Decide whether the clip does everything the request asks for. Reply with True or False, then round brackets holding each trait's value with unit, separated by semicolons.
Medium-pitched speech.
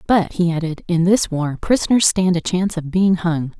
True (175 Hz)